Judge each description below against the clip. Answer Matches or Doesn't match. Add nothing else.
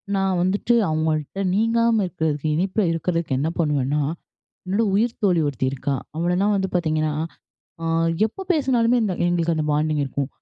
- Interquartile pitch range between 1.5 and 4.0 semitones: Doesn't match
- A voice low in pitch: Doesn't match